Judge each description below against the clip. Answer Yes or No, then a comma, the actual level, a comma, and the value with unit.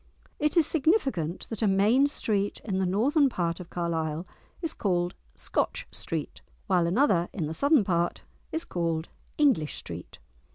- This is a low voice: No, high, 195 Hz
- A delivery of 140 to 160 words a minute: Yes, average, 155 wpm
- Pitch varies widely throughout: Yes, wide, 8.5 semitones